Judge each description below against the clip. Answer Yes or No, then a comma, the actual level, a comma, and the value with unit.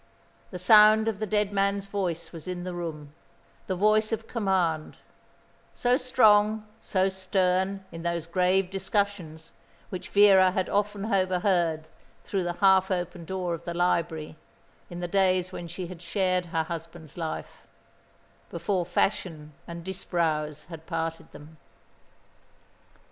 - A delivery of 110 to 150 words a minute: Yes, average, 140 wpm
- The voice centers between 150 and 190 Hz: Yes, medium, 185 Hz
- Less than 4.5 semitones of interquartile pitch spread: Yes, average, 2.7 semitones